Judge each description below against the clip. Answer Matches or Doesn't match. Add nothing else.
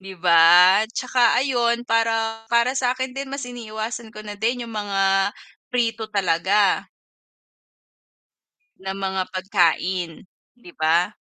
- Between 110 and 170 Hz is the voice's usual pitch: Doesn't match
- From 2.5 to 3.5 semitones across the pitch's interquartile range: Doesn't match